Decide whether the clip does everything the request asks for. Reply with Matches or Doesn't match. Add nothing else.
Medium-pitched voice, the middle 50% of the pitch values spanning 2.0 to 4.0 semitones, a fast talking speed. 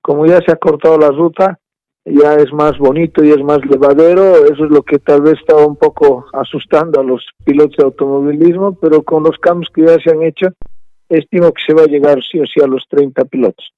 Matches